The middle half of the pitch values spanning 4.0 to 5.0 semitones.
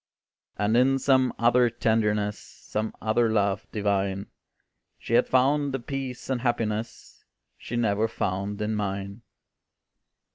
No: average, 3.2 semitones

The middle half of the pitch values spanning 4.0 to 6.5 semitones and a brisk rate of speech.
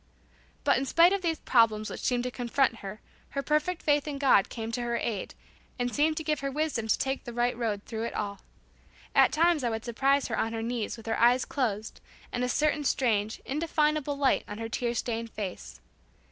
Yes: average, 4.3 semitones; fast, 215 wpm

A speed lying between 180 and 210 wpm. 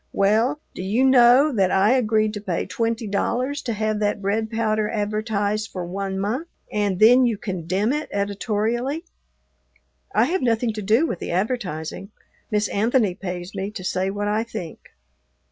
No: average, 165 wpm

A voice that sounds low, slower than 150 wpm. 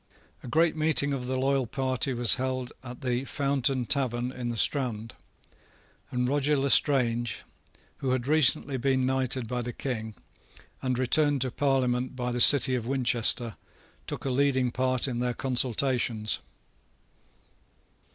Yes: low, 130 Hz; average, 140 wpm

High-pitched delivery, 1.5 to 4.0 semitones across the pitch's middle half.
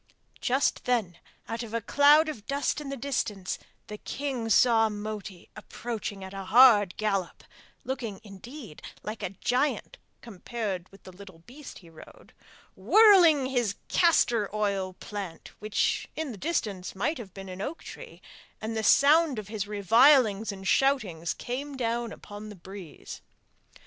No: high, 220 Hz; average, 5.1 semitones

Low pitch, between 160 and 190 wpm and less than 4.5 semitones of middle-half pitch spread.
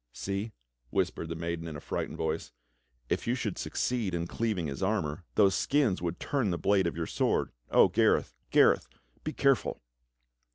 No: very low, 95 Hz; average, 170 wpm; average, 4.9 semitones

